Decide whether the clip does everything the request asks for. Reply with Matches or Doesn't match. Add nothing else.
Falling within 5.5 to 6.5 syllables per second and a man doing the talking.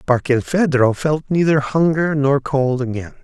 Doesn't match